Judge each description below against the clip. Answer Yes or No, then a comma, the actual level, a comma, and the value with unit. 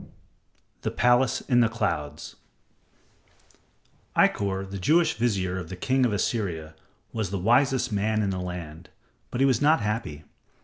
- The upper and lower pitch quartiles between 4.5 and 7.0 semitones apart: Yes, average, 5.0 semitones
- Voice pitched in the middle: No, low, 105 Hz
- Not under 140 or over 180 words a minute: Yes, average, 150 wpm